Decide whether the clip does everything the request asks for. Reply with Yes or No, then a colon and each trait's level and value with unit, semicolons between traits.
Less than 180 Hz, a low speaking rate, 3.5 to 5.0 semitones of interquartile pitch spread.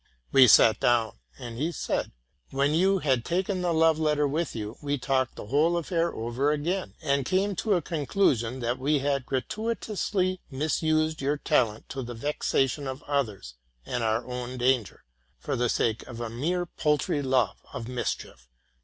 No: medium, 140 Hz; average, 175 wpm; average, 4.7 semitones